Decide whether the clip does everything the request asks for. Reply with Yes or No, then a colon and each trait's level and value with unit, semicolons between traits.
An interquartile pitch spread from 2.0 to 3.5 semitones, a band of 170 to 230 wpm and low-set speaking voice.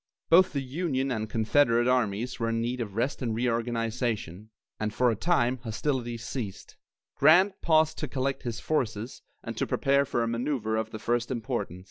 Yes: average, 3.2 semitones; average, 175 wpm; low, 120 Hz